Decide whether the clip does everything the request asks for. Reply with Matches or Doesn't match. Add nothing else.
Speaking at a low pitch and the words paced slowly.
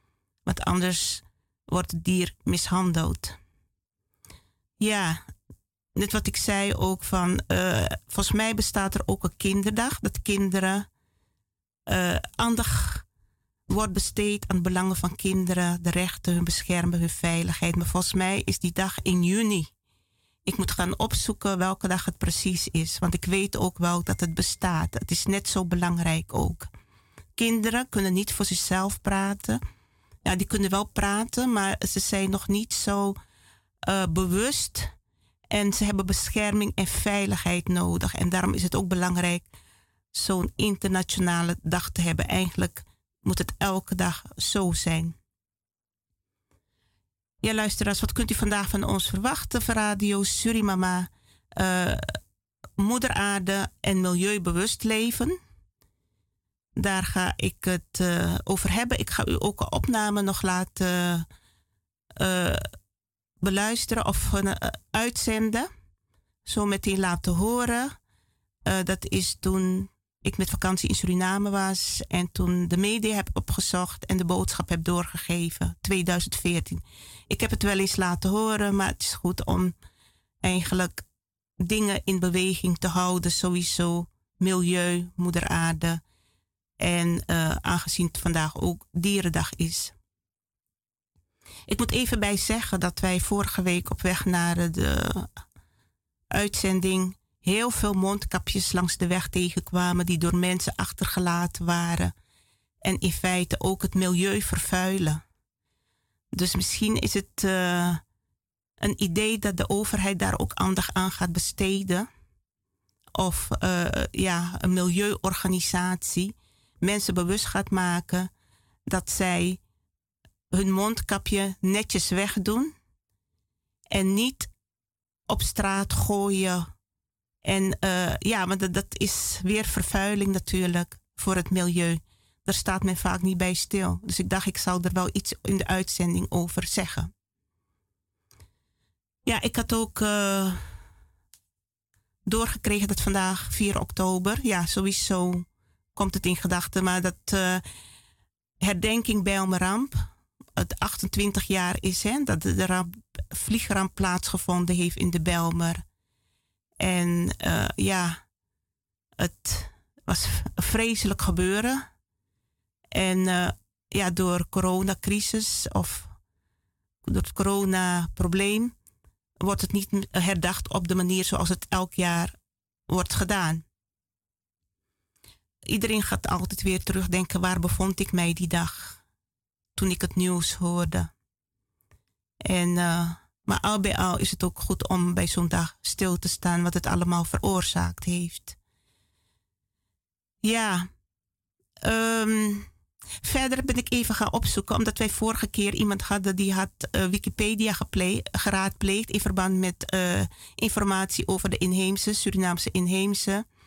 Doesn't match